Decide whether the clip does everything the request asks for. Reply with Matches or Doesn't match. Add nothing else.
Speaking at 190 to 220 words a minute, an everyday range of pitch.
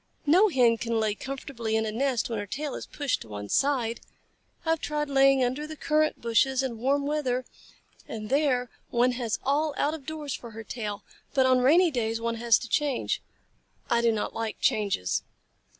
Matches